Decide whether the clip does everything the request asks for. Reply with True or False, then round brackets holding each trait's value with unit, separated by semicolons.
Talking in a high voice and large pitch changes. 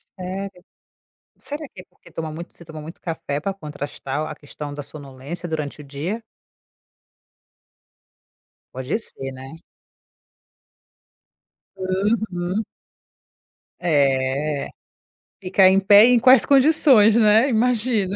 False (180 Hz; 6.2 semitones)